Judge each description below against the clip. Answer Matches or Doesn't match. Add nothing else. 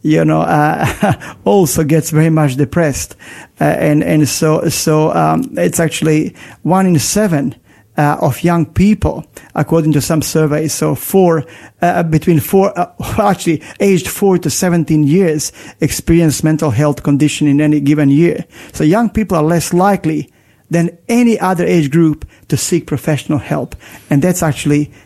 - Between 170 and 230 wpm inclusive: Doesn't match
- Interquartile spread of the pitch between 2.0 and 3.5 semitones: Matches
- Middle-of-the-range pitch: Matches